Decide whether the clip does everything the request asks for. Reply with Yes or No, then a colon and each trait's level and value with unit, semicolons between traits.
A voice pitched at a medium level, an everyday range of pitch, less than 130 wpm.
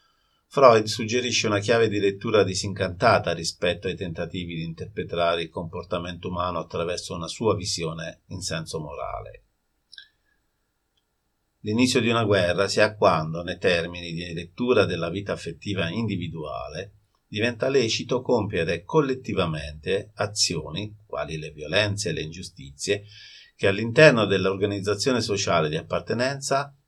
No: low, 100 Hz; average, 4.9 semitones; average, 120 wpm